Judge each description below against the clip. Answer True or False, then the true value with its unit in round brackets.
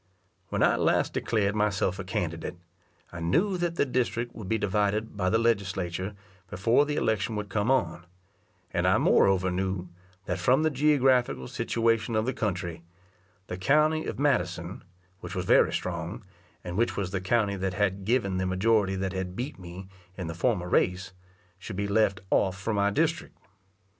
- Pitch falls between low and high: False (100 Hz)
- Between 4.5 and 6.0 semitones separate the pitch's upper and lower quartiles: False (4.0 semitones)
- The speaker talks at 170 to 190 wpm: True (175 wpm)